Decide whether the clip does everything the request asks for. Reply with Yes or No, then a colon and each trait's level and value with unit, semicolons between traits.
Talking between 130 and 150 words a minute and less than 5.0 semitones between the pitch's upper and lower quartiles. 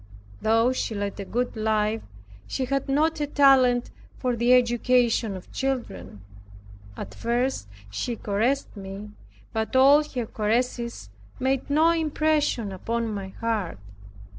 Yes: slow, 135 wpm; average, 4.1 semitones